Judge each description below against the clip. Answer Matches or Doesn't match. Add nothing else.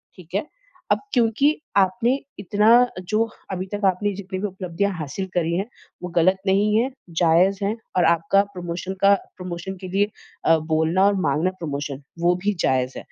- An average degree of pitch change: Matches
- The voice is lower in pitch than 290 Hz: Matches